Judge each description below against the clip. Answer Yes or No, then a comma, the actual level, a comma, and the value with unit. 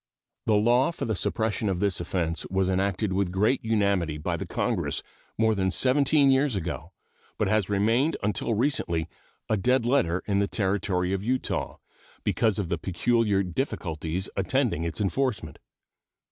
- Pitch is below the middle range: Yes, low, 100 Hz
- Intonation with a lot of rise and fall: No, average, 4.2 semitones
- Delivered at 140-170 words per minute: Yes, average, 150 wpm